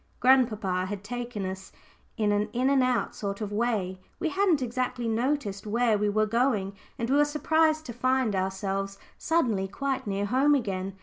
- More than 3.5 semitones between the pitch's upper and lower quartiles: Yes, average, 4.7 semitones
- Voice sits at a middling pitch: No, high, 230 Hz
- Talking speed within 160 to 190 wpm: Yes, average, 170 wpm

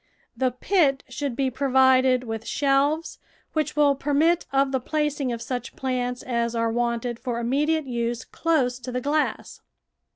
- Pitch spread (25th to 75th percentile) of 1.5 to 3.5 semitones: Yes, average, 2.8 semitones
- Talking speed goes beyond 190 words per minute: No, average, 155 wpm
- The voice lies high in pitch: Yes, very high, 260 Hz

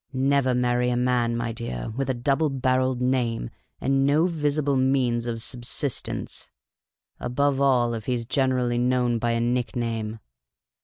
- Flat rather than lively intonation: Yes, narrow, 2.1 semitones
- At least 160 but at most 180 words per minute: No, average, 150 wpm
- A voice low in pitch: Yes, low, 125 Hz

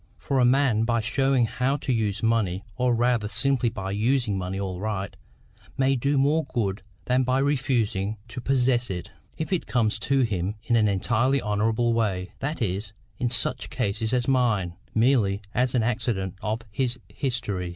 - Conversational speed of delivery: Yes, average, 170 wpm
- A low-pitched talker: Yes, low, 115 Hz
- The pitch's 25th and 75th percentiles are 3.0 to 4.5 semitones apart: Yes, average, 3.8 semitones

